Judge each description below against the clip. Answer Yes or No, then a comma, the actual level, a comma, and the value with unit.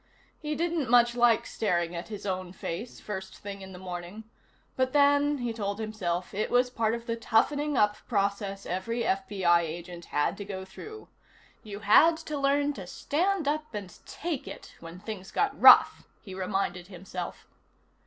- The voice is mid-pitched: No, high, 210 Hz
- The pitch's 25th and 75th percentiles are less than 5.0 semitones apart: No, wide, 5.6 semitones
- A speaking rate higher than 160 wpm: Yes, average, 170 wpm